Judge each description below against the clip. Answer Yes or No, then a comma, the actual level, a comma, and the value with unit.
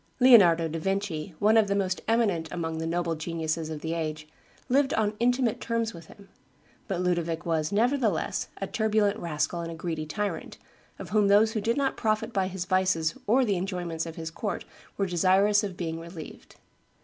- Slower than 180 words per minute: No, average, 185 wpm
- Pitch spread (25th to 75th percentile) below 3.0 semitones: No, average, 4.4 semitones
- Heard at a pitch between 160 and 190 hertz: Yes, medium, 185 Hz